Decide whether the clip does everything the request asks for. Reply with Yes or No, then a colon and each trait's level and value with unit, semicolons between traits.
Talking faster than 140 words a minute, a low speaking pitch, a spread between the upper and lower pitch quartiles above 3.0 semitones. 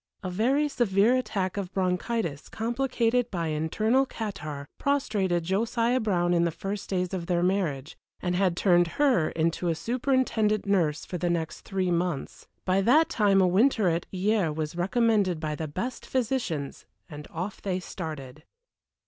No: average, 155 wpm; high, 190 Hz; average, 4.8 semitones